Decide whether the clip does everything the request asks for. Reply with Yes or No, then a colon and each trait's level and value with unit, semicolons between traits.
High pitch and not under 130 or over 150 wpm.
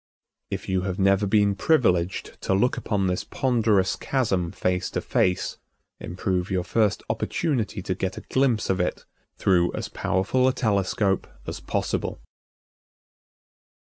No: very low, 95 Hz; average, 140 wpm